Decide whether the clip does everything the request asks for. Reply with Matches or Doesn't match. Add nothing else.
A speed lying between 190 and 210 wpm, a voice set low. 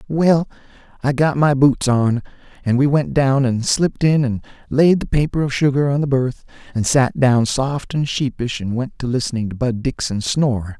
Matches